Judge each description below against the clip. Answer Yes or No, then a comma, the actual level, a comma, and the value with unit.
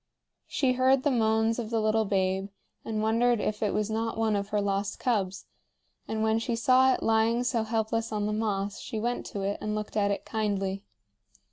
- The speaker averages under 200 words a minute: No, fast, 205 wpm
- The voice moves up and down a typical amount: No, narrow, 1.9 semitones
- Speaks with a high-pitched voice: Yes, high, 220 Hz